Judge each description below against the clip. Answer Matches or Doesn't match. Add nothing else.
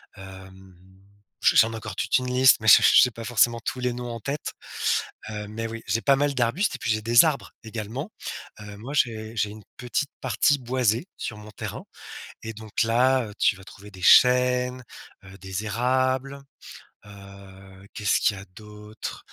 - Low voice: Matches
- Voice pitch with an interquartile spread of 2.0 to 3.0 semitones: Doesn't match